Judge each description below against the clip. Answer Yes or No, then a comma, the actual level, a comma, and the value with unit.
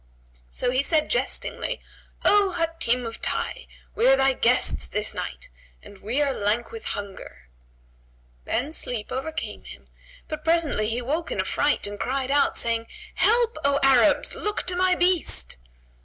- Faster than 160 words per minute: No, average, 155 wpm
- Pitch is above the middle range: Yes, very high, 275 Hz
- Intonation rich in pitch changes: Yes, wide, 6.4 semitones